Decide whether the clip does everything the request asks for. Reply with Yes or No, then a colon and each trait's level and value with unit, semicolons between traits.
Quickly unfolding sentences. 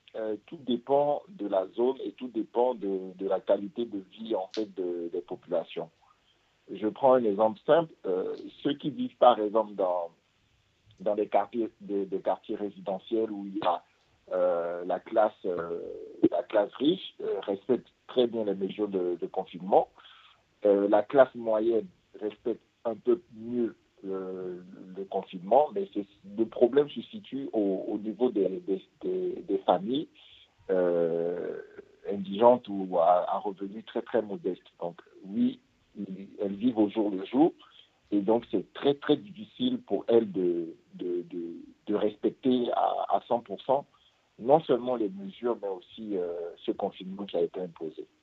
No: average, 160 wpm